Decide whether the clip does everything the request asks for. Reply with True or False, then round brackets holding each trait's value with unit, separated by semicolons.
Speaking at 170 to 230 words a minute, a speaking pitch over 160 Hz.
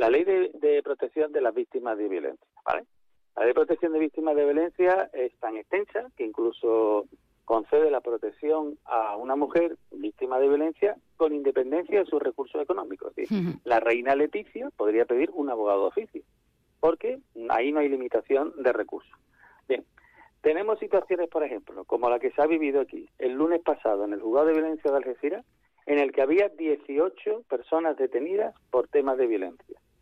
True (180 wpm; 185 Hz)